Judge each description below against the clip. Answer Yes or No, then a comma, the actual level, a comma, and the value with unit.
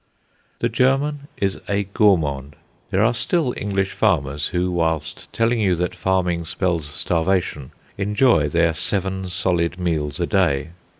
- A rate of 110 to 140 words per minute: Yes, slow, 135 wpm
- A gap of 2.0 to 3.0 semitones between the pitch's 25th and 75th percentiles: No, average, 3.8 semitones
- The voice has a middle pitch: No, very low, 90 Hz